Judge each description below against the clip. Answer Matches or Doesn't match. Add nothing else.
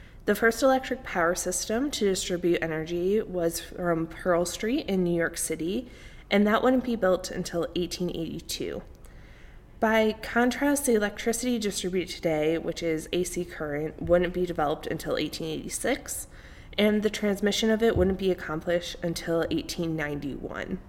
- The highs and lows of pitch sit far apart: Doesn't match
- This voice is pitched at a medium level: Matches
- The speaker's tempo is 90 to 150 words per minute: Matches